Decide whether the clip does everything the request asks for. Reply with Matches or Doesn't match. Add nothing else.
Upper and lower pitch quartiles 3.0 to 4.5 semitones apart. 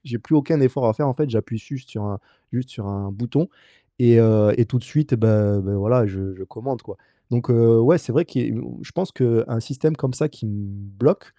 Matches